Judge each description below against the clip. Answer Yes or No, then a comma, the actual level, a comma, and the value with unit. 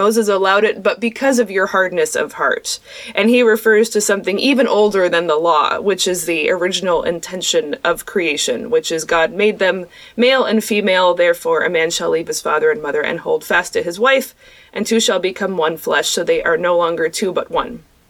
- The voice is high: Yes, high, 210 Hz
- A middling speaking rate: No, fast, 210 wpm